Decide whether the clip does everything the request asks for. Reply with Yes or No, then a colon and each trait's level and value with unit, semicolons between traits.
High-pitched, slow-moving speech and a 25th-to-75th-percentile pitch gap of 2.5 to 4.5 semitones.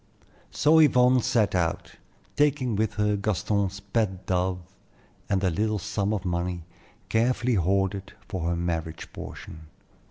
No: low, 100 Hz; slow, 130 wpm; average, 3.7 semitones